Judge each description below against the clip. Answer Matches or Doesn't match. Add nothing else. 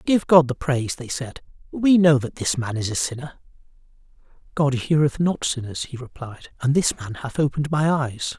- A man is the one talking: Matches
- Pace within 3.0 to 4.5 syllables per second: Doesn't match